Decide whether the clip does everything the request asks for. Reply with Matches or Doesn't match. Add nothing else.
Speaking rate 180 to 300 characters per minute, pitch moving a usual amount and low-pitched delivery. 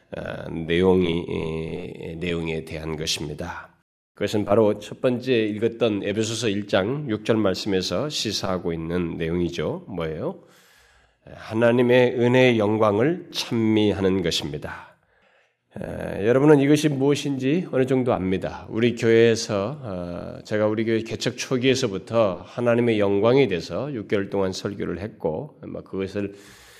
Matches